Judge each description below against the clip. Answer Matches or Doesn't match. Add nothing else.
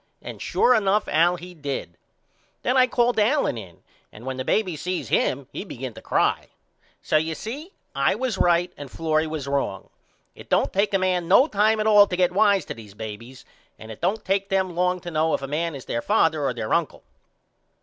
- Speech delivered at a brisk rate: Matches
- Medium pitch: Matches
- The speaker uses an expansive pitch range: Matches